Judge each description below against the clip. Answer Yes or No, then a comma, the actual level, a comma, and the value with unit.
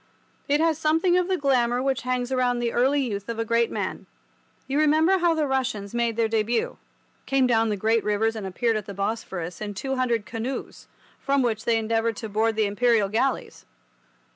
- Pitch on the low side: No, high, 235 Hz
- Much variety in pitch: No, average, 3.5 semitones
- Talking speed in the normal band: Yes, average, 190 wpm